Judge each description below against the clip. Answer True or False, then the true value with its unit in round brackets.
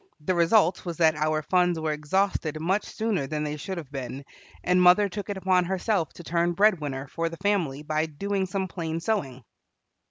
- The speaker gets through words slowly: False (195 wpm)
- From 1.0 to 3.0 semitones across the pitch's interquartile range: False (3.8 semitones)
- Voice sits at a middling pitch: True (170 Hz)